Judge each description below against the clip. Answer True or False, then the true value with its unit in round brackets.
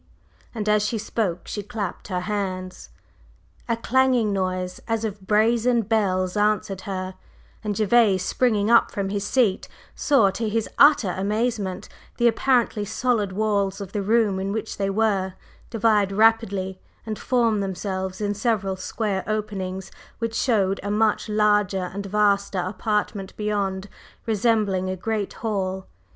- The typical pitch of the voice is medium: False (205 Hz)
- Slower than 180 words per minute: True (140 wpm)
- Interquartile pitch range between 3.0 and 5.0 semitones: False (2.6 semitones)